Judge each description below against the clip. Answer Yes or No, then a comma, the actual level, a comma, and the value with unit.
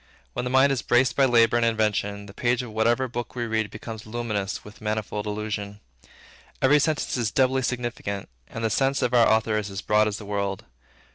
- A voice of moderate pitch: No, low, 110 Hz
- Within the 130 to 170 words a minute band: No, fast, 205 wpm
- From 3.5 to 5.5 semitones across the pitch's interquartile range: No, average, 2.8 semitones